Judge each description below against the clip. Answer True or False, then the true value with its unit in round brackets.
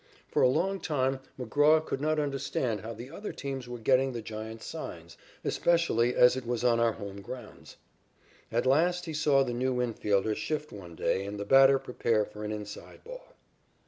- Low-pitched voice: True (125 Hz)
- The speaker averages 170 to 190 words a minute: True (185 wpm)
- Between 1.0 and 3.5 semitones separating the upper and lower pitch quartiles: False (4.7 semitones)